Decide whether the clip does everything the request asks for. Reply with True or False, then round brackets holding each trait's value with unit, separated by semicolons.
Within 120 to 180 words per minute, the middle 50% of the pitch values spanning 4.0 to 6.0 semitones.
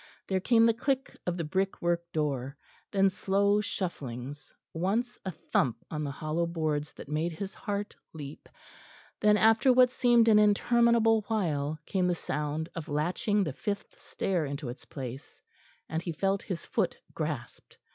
True (155 wpm; 5.5 semitones)